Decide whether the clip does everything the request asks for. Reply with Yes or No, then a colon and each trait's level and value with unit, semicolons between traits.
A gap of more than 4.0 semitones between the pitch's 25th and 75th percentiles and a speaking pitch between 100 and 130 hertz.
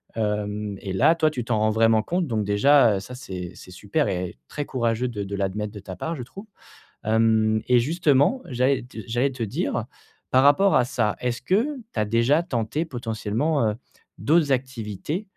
Yes: average, 5.2 semitones; low, 120 Hz